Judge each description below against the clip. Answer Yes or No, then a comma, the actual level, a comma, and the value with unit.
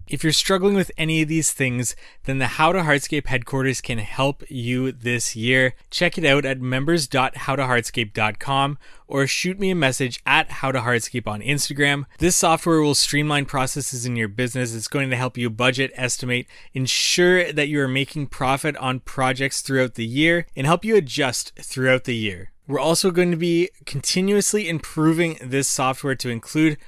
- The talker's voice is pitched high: No, low, 135 Hz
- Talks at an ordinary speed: Yes, average, 170 wpm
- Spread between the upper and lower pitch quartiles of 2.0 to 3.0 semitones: No, average, 3.7 semitones